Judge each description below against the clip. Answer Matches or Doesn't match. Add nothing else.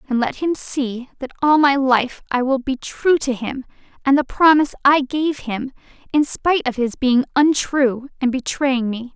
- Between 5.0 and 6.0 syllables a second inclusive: Doesn't match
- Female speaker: Matches